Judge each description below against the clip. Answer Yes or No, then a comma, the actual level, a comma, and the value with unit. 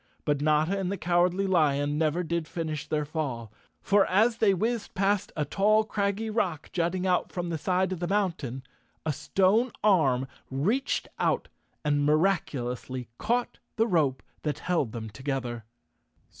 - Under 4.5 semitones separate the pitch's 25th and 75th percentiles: No, average, 5.2 semitones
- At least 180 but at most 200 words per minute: No, average, 150 wpm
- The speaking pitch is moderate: Yes, medium, 170 Hz